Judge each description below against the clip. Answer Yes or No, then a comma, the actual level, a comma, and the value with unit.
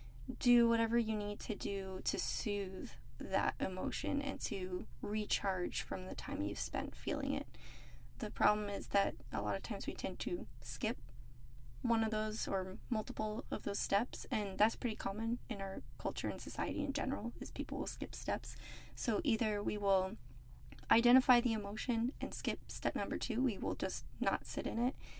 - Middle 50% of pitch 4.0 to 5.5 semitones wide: No, average, 2.9 semitones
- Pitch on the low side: No, high, 220 Hz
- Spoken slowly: No, average, 180 wpm